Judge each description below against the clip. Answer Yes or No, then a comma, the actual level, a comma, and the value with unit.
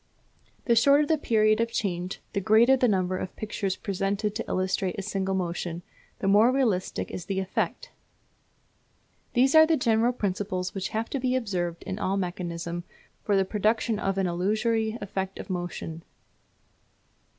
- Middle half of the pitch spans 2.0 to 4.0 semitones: Yes, average, 3.6 semitones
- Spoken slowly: No, average, 160 wpm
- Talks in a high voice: Yes, high, 200 Hz